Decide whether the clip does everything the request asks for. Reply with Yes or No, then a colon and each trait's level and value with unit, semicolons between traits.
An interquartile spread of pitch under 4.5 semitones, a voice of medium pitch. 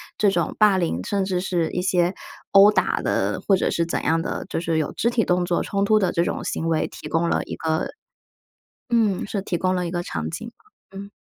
Yes: average, 2.9 semitones; medium, 180 Hz